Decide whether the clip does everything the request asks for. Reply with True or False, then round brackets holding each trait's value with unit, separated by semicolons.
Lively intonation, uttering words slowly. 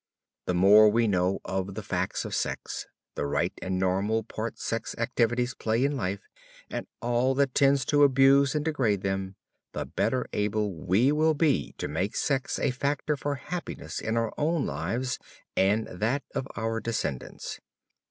False (5.7 semitones; 165 wpm)